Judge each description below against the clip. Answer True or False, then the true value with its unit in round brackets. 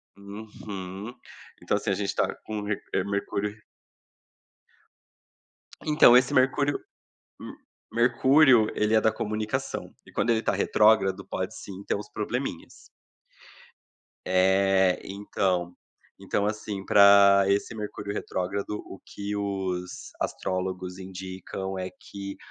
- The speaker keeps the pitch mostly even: True (2.1 semitones)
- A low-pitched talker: True (100 Hz)